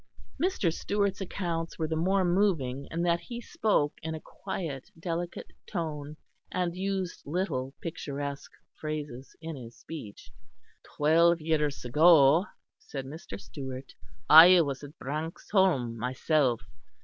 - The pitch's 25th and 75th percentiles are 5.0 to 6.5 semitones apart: No, average, 4.0 semitones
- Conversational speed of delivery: No, slow, 125 wpm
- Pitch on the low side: No, medium, 160 Hz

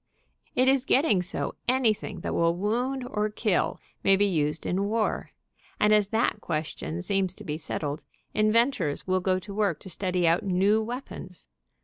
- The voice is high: Yes, high, 200 Hz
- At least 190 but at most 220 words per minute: No, average, 165 wpm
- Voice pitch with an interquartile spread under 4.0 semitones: Yes, average, 3.6 semitones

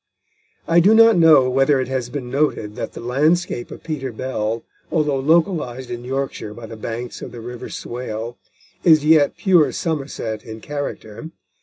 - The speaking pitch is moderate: No, low, 130 Hz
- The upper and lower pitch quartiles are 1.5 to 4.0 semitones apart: No, average, 4.5 semitones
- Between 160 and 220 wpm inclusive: Yes, average, 165 wpm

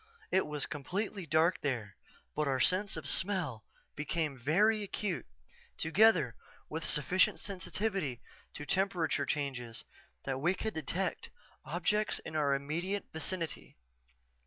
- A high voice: No, medium, 160 Hz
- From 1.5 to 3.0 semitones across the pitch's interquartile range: No, average, 5.3 semitones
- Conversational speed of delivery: No, slow, 120 wpm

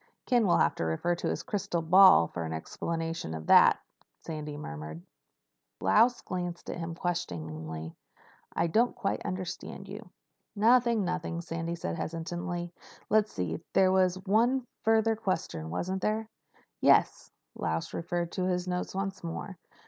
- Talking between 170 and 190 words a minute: No, average, 140 wpm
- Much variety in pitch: No, average, 4.4 semitones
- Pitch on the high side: No, medium, 175 Hz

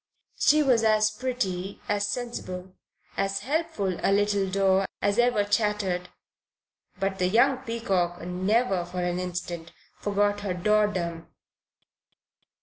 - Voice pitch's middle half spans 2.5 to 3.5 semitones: Yes, average, 3.0 semitones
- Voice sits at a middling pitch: No, high, 200 Hz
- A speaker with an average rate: No, slow, 125 wpm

